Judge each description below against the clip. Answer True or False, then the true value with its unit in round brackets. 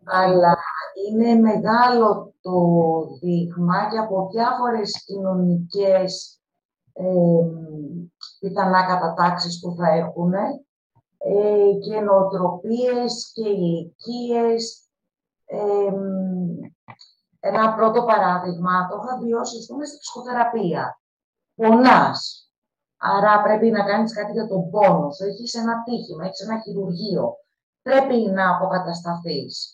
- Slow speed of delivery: True (100 wpm)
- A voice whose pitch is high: True (200 Hz)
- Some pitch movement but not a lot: True (3.9 semitones)